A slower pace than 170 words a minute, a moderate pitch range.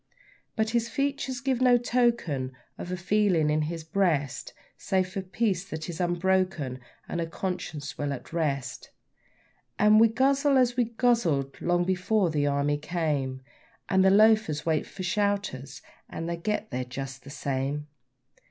No: average, 155 wpm; wide, 6.6 semitones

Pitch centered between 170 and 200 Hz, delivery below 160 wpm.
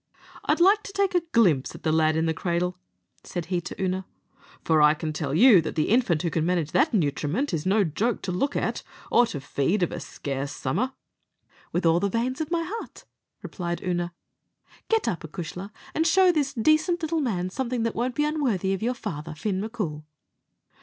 No: high, 190 Hz; average, 200 wpm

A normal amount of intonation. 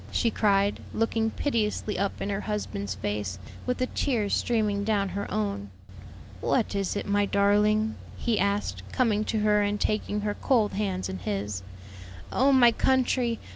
No: narrow, 2.1 semitones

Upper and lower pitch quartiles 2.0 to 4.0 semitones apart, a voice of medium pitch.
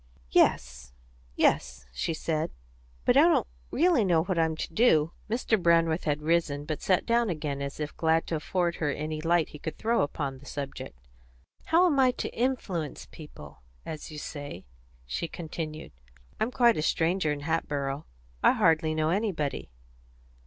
Yes: average, 3.4 semitones; medium, 160 Hz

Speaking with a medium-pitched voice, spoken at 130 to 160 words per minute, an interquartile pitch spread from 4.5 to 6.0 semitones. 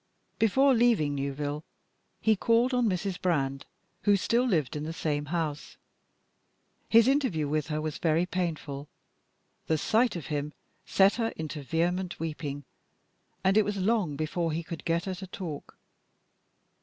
Yes: medium, 170 Hz; average, 150 wpm; average, 5.2 semitones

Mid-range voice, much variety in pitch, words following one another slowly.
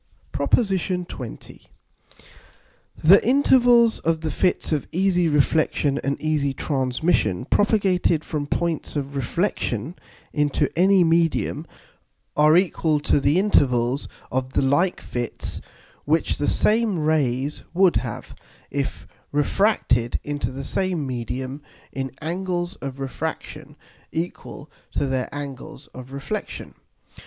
No: medium, 150 Hz; average, 4.8 semitones; slow, 115 wpm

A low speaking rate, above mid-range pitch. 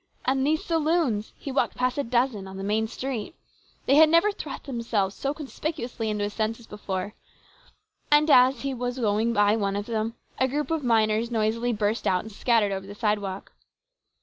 No: average, 185 wpm; high, 230 Hz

